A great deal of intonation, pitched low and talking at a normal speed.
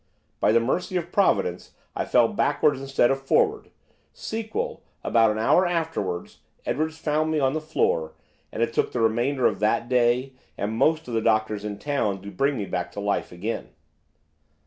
Yes: wide, 6.4 semitones; low, 125 Hz; average, 180 wpm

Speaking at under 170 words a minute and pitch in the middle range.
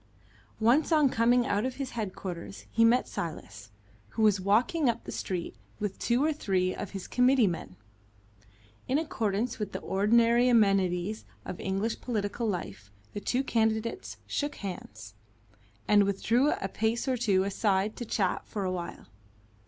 No: average, 155 wpm; high, 215 Hz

